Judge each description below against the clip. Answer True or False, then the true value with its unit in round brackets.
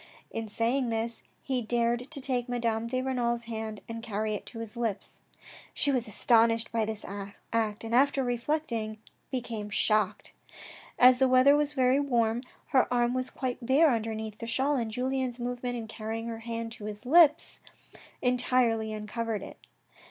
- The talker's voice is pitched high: True (235 Hz)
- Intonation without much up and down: True (2.3 semitones)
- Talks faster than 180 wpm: False (165 wpm)